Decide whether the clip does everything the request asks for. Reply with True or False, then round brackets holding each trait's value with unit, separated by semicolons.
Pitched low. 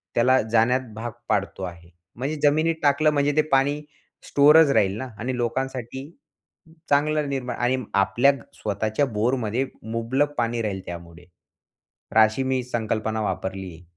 True (120 Hz)